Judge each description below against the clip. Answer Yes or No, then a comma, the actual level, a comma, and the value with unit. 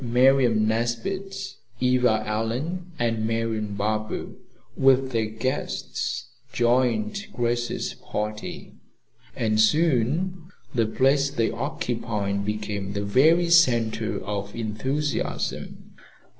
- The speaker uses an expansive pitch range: No, average, 3.8 semitones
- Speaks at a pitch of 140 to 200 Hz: No, low, 115 Hz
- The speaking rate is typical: No, slow, 90 wpm